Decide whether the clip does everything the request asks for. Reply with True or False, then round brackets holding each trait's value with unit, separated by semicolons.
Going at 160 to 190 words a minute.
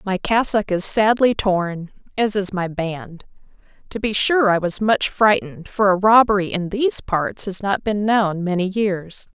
True (180 wpm)